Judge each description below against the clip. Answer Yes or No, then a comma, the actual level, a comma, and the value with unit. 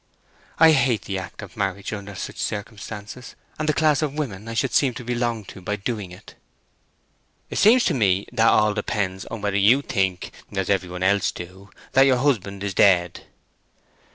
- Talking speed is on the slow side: No, average, 180 wpm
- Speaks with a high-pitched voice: No, low, 105 Hz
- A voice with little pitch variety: No, average, 4.3 semitones